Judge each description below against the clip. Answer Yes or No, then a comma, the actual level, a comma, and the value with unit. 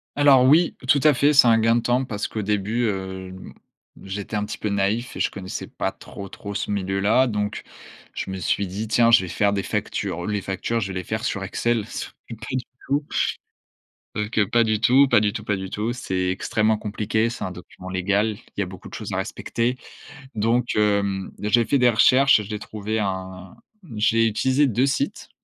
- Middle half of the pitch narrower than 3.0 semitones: No, average, 3.3 semitones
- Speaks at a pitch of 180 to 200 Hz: No, low, 105 Hz